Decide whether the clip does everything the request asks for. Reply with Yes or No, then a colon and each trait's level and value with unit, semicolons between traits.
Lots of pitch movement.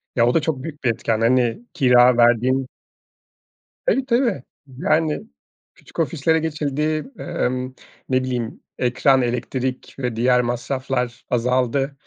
No: average, 3.3 semitones